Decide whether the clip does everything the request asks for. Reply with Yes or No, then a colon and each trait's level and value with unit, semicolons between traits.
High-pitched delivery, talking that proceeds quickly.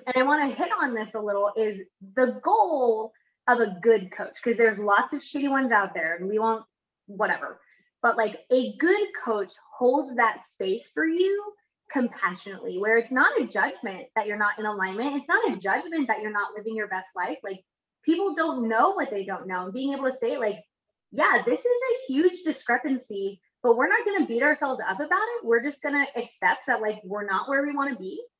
Yes: high, 245 Hz; fast, 215 wpm